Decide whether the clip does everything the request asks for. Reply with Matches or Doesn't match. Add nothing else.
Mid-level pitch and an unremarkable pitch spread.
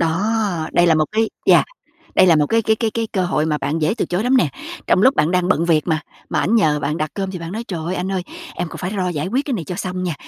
Matches